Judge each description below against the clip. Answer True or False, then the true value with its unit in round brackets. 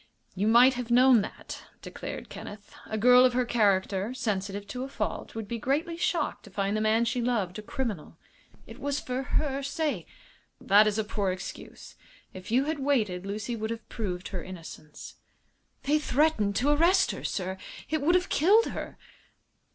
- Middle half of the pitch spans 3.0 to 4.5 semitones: False (5.2 semitones)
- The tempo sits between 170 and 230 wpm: True (180 wpm)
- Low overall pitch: False (230 Hz)